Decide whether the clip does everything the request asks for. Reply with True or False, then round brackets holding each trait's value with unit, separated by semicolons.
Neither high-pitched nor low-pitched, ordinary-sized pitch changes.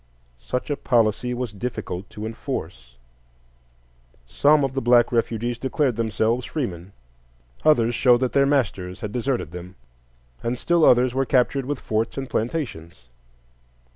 False (120 Hz; 3.9 semitones)